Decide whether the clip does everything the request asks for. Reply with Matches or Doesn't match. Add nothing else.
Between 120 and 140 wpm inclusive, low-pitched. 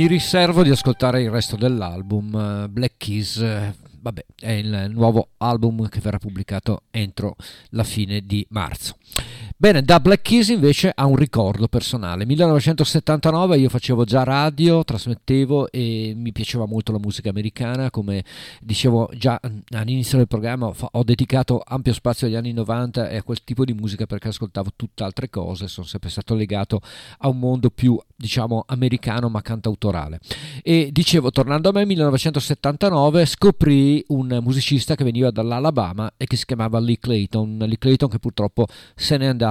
Doesn't match